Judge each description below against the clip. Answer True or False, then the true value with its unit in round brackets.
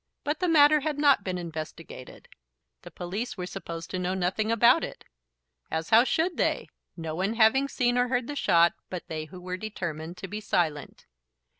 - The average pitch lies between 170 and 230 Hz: True (190 Hz)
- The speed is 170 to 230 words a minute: True (185 wpm)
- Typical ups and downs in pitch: False (6.4 semitones)